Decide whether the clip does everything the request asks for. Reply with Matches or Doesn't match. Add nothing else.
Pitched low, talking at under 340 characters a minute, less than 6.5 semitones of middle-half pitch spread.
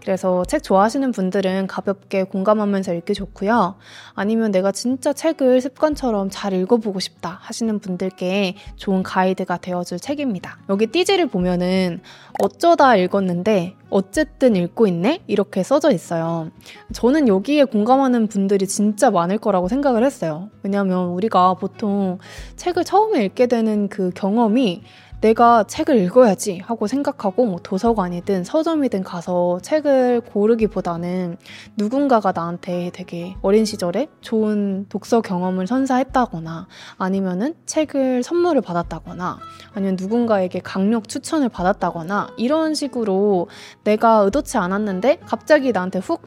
Doesn't match